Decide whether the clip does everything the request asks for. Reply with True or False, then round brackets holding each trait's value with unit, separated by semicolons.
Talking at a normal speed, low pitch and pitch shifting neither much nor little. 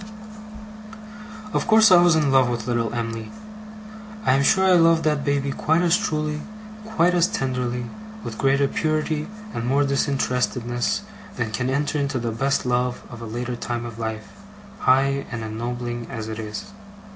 True (165 wpm; 130 Hz; 4.3 semitones)